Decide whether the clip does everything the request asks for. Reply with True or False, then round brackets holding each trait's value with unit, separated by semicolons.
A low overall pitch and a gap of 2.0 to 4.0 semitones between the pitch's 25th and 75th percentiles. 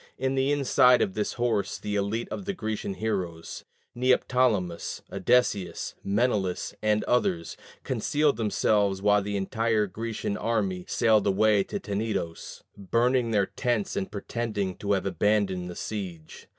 True (105 Hz; 3.3 semitones)